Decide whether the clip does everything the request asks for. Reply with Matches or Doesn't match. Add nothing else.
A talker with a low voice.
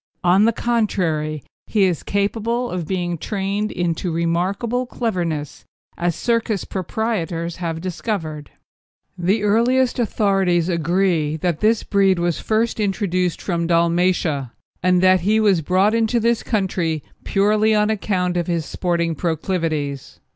Doesn't match